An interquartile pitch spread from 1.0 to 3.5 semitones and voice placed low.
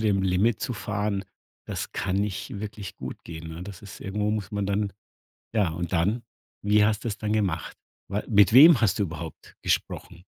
Yes: narrow, 2.4 semitones; low, 100 Hz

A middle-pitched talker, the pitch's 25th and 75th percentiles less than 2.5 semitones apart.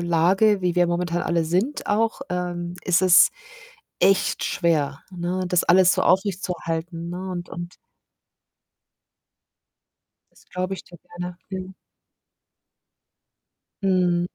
Yes: medium, 180 Hz; narrow, 1.4 semitones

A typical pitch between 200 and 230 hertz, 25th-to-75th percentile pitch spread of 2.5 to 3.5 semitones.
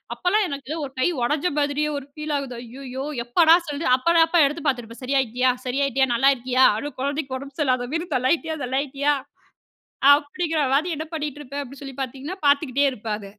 No: very high, 280 Hz; average, 2.8 semitones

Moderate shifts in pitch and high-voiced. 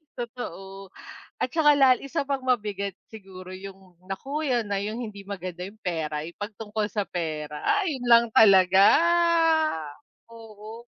Yes: average, 4.1 semitones; high, 205 Hz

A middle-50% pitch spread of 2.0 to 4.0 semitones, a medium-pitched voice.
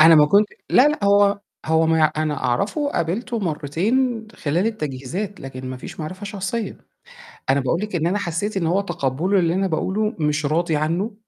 No: average, 4.9 semitones; medium, 175 Hz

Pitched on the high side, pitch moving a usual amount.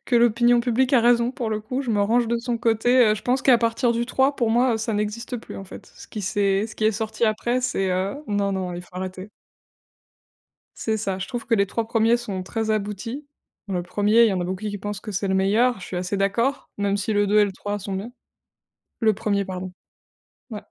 Yes: high, 215 Hz; average, 3.0 semitones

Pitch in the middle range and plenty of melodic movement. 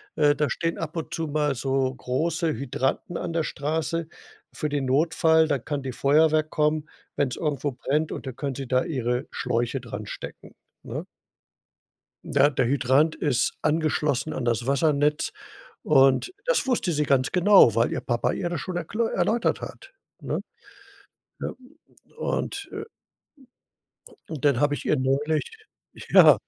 No: medium, 145 Hz; average, 3.3 semitones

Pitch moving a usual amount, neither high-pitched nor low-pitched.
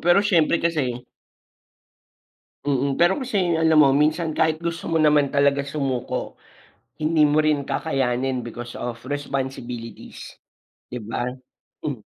Yes: average, 3.8 semitones; medium, 145 Hz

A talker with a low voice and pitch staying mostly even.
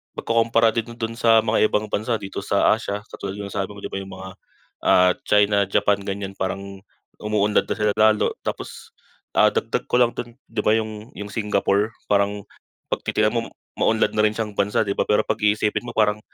Yes: low, 105 Hz; narrow, 1.8 semitones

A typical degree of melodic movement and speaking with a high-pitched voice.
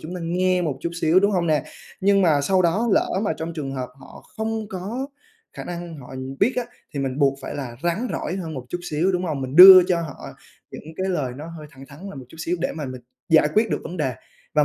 No: average, 4.4 semitones; medium, 170 Hz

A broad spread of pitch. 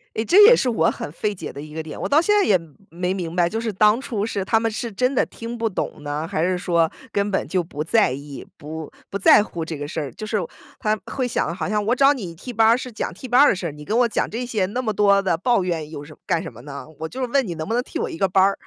Yes: wide, 6.0 semitones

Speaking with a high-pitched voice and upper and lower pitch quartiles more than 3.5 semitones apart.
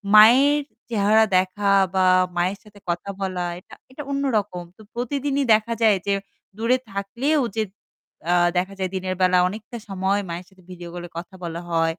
Yes: high, 200 Hz; average, 4.1 semitones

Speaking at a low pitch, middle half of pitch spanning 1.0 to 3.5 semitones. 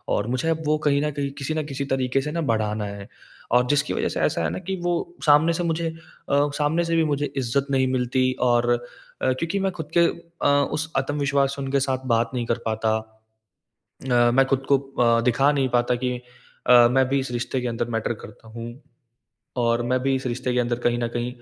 Yes: low, 130 Hz; average, 3.2 semitones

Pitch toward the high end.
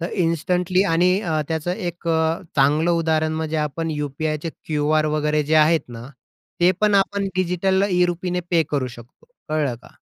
No: medium, 160 Hz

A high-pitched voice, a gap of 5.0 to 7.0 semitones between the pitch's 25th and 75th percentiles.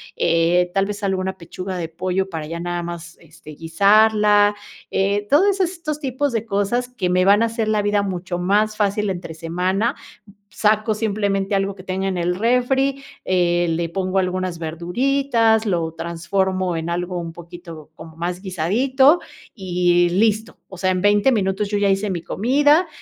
No: high, 195 Hz; average, 3.6 semitones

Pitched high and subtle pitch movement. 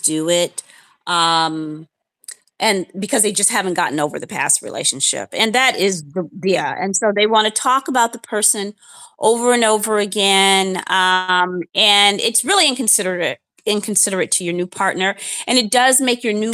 No: high, 200 Hz; average, 3.3 semitones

